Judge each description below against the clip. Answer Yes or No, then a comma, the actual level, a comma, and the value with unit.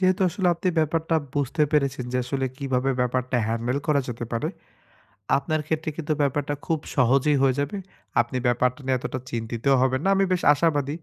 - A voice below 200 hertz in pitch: Yes, medium, 140 Hz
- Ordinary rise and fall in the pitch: Yes, average, 3.7 semitones